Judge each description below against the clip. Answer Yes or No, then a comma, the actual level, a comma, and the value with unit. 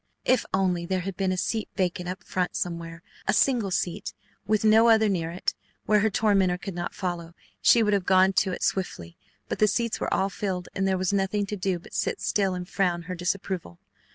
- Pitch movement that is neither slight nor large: No, narrow, 2.3 semitones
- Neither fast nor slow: No, fast, 215 wpm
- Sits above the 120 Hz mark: Yes, high, 190 Hz